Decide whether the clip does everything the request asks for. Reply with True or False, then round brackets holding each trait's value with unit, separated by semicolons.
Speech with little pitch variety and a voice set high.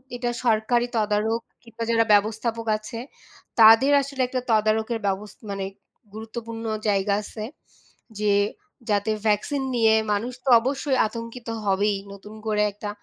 True (2.0 semitones; 220 Hz)